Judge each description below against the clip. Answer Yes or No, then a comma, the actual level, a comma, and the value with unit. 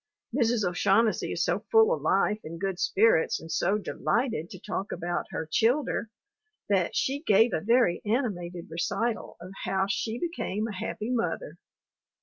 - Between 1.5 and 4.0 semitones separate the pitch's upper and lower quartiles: No, average, 5.0 semitones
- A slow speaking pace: No, average, 155 wpm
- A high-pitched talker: Yes, high, 210 Hz